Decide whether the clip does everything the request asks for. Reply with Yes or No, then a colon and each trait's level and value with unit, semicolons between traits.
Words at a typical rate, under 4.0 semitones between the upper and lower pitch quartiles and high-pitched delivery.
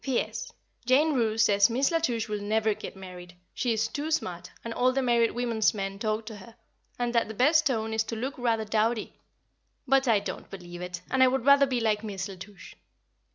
No: fast, 220 wpm; average, 3.5 semitones; high, 225 Hz